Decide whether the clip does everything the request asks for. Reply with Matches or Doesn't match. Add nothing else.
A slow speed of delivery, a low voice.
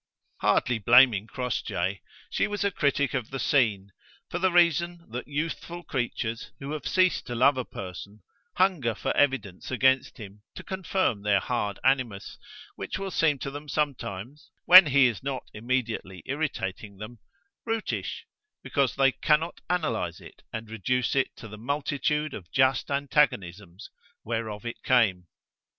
Doesn't match